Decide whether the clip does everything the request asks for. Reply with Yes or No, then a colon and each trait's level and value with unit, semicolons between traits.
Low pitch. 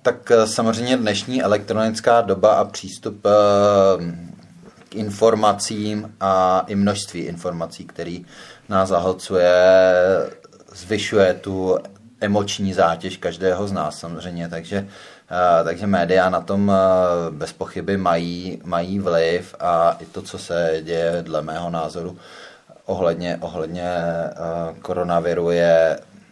Yes: very low, 95 Hz